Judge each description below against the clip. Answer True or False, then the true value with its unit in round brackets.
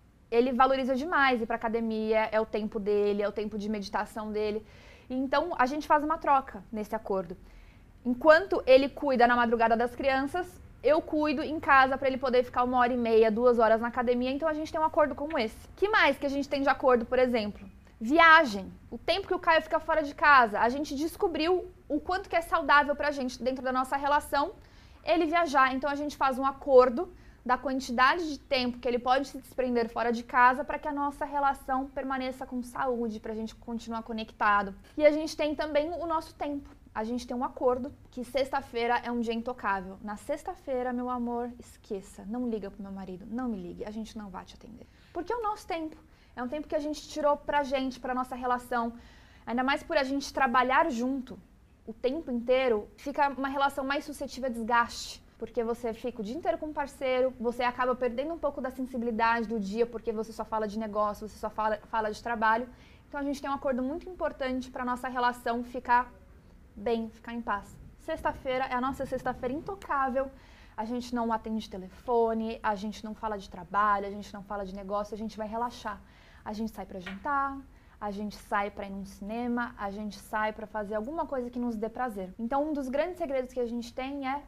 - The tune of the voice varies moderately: True (4.2 semitones)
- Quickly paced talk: True (215 wpm)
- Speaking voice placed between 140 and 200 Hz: False (255 Hz)